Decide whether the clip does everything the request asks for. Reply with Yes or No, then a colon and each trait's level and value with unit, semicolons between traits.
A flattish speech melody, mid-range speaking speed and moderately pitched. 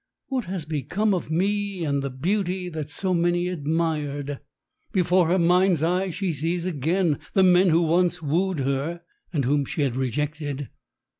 No: average, 3.8 semitones; average, 160 wpm; medium, 170 Hz